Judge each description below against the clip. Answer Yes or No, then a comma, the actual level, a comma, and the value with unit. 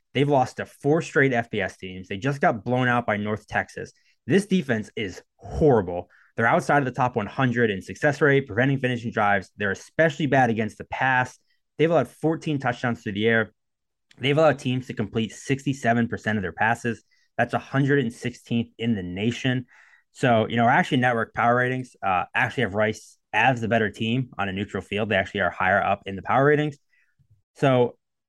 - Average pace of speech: Yes, average, 185 wpm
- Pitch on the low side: Yes, low, 120 Hz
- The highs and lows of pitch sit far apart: No, average, 3.9 semitones